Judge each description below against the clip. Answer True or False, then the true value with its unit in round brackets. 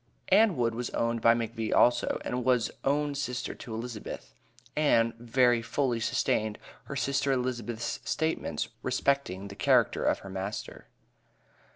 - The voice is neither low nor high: False (120 Hz)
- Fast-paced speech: False (140 wpm)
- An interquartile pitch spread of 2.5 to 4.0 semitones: True (3.2 semitones)